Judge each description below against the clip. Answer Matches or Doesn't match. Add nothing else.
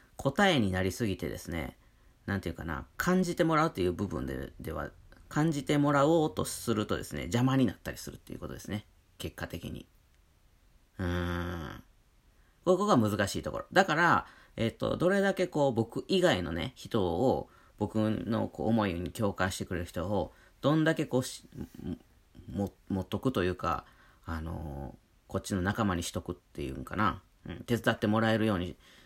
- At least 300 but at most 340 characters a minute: Matches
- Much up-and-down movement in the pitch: Matches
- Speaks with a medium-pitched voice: Doesn't match